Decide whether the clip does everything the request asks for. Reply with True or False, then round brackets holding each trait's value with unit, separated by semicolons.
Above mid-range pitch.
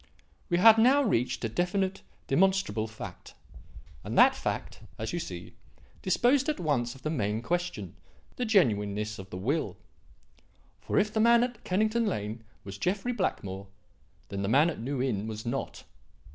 False (140 Hz)